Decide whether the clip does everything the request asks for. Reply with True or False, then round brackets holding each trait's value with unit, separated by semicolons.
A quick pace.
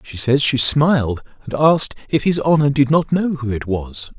True (215 wpm)